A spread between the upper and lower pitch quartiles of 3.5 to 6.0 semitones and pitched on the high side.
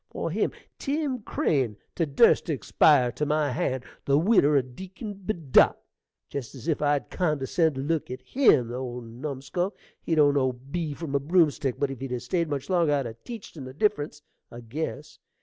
No: average, 4.3 semitones; medium, 145 Hz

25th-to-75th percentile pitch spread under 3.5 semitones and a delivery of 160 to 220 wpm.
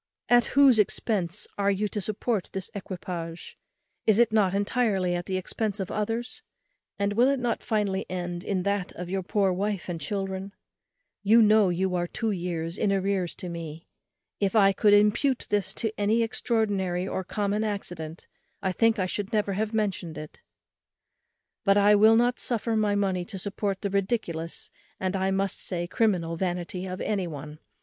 Yes: average, 2.8 semitones; average, 175 wpm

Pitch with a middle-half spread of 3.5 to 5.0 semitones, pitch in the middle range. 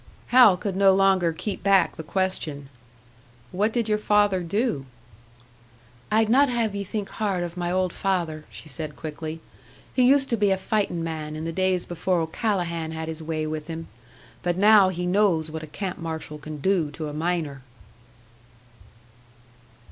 Yes: average, 4.0 semitones; medium, 180 Hz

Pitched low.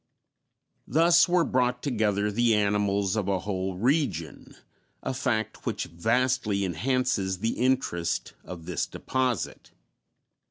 Yes: low, 110 Hz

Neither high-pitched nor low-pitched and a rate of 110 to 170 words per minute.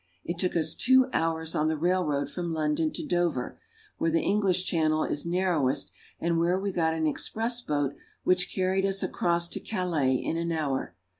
No: medium, 170 Hz; average, 190 wpm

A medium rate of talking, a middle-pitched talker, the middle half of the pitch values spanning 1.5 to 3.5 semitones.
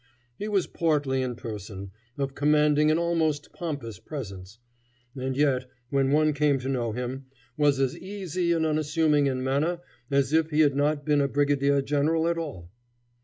Yes: average, 170 wpm; medium, 145 Hz; average, 2.8 semitones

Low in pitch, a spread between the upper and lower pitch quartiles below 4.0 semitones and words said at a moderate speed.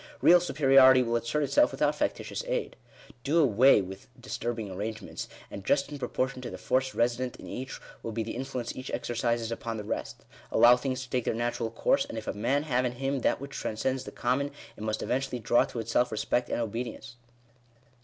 No: low, 125 Hz; narrow, 2.6 semitones; fast, 215 wpm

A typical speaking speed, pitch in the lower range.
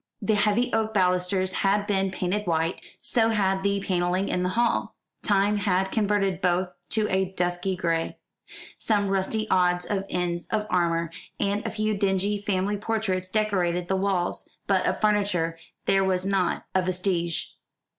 No: average, 155 wpm; high, 190 Hz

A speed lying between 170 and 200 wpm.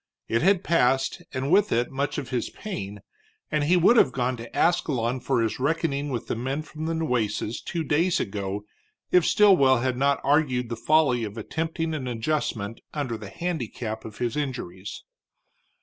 Yes: average, 175 wpm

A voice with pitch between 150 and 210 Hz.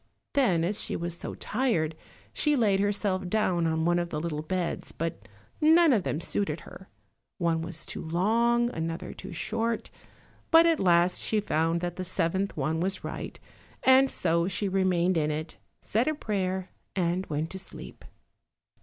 Yes: medium, 185 Hz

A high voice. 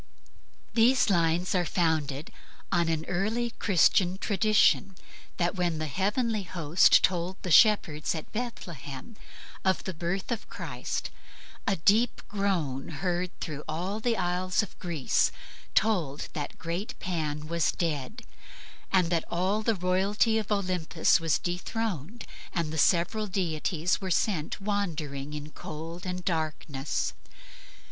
No: medium, 180 Hz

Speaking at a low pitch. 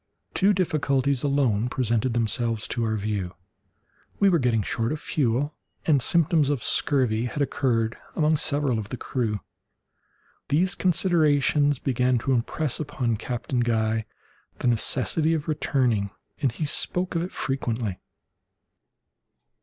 Yes: low, 130 Hz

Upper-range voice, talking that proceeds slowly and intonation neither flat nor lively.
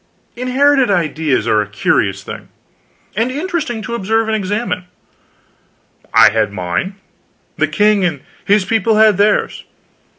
No: high, 210 Hz; slow, 130 wpm; wide, 6.5 semitones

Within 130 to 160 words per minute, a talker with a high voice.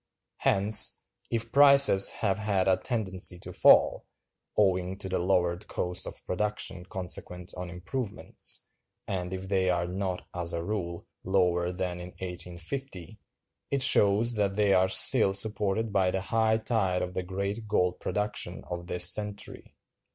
No: average, 145 wpm; very low, 95 Hz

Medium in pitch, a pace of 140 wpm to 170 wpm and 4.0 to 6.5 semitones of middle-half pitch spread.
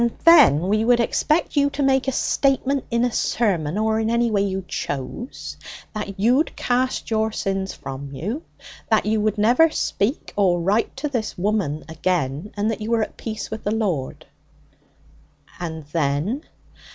No: high, 215 Hz; average, 165 wpm; average, 4.8 semitones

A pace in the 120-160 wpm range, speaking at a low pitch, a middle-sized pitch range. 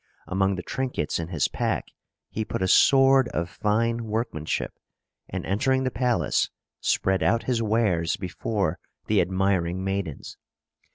Yes: slow, 135 wpm; low, 100 Hz; average, 4.5 semitones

